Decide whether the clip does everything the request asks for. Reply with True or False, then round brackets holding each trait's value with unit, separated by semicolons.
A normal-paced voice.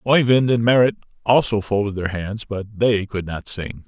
True (185 wpm)